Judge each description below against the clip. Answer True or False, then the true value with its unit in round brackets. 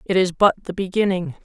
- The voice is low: False (190 Hz)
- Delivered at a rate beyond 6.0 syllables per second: True (6.3 syllables/s)